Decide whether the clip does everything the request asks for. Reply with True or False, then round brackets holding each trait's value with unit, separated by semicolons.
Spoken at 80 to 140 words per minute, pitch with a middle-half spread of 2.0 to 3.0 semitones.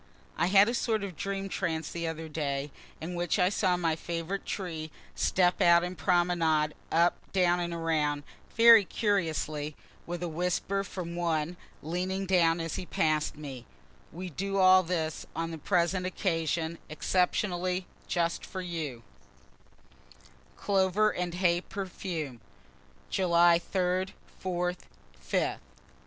True (135 wpm; 2.4 semitones)